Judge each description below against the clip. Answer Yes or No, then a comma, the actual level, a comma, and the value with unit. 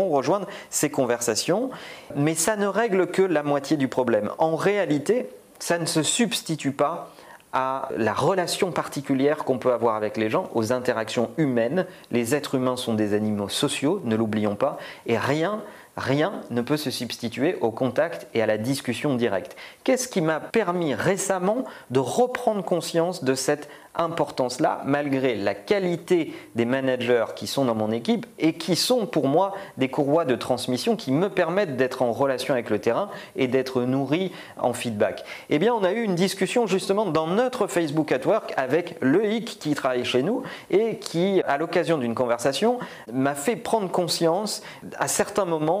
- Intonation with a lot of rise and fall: Yes, wide, 6.8 semitones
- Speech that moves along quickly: No, average, 175 wpm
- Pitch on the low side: No, medium, 150 Hz